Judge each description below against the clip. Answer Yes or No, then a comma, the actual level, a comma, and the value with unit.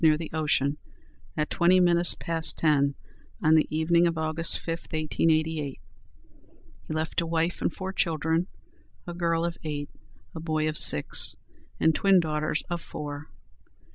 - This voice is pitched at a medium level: Yes, medium, 160 Hz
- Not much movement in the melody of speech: Yes, narrow, 1.6 semitones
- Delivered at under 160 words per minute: Yes, average, 150 wpm